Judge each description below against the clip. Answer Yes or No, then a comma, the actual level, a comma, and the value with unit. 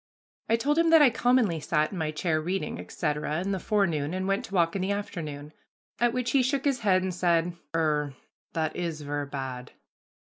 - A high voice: No, medium, 175 Hz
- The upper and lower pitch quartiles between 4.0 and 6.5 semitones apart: Yes, wide, 5.5 semitones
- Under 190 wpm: No, fast, 205 wpm